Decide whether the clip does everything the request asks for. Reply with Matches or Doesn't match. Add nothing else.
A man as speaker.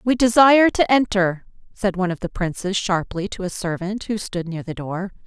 Doesn't match